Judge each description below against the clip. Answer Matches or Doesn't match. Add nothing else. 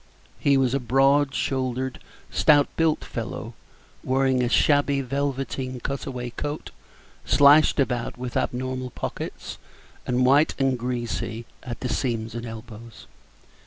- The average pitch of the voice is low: Matches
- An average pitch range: Doesn't match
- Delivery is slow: Matches